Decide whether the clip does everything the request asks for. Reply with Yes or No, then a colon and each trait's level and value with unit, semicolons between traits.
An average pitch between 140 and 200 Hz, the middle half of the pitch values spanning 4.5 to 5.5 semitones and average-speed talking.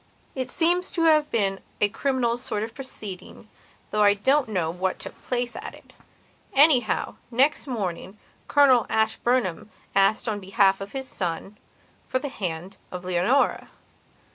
No: high, 220 Hz; average, 5.2 semitones; average, 145 wpm